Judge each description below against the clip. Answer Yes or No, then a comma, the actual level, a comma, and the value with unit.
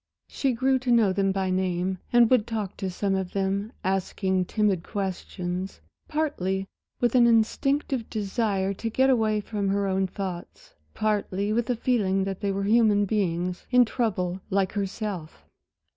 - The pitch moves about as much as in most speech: Yes, average, 3.1 semitones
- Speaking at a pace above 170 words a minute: No, average, 160 wpm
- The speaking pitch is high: Yes, high, 200 Hz